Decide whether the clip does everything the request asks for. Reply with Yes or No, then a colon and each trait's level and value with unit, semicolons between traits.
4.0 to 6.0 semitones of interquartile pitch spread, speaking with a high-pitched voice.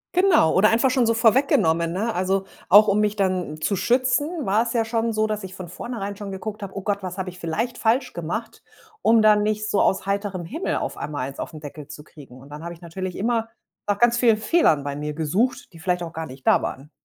Yes: average, 5.0 semitones; high, 200 Hz